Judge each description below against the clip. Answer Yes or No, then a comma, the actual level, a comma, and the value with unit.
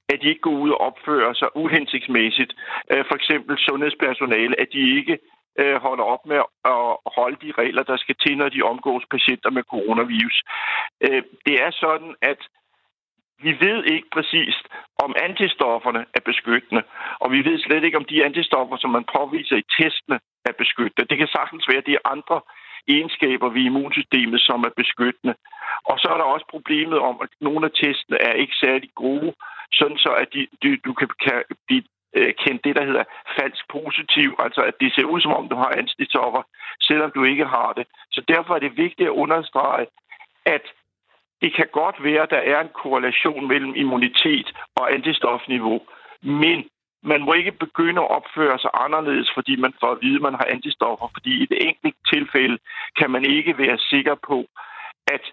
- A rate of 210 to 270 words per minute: No, average, 175 wpm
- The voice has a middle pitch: Yes, medium, 165 Hz